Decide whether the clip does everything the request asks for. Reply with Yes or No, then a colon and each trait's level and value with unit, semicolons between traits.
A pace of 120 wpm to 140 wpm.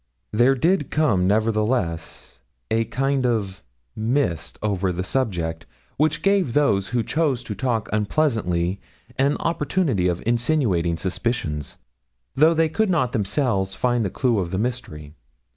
Yes: slow, 135 wpm